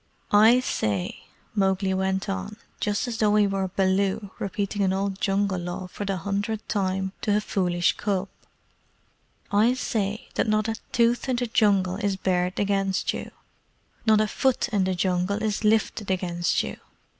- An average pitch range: No, narrow, 2.0 semitones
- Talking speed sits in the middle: Yes, average, 165 wpm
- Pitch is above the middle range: Yes, high, 200 Hz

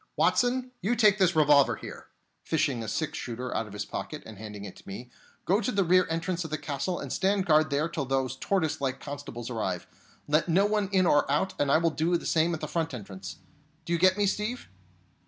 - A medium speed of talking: No, fast, 230 wpm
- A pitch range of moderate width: No, wide, 6.0 semitones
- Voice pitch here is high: No, medium, 155 Hz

